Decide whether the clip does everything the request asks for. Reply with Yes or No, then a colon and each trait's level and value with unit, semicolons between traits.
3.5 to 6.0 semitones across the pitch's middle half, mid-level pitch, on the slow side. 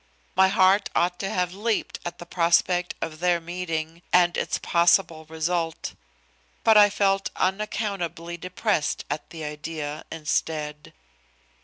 No: average, 2.7 semitones; medium, 175 Hz; slow, 130 wpm